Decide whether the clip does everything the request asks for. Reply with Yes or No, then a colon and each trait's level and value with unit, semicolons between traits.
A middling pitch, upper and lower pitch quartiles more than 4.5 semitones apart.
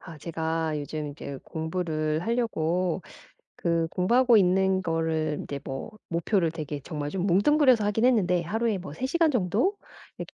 Yes: medium, 175 Hz; average, 5.2 semitones